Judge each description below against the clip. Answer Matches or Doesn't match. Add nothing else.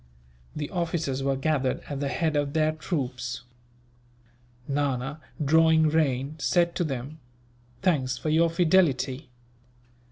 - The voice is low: Doesn't match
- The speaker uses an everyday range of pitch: Matches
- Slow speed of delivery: Matches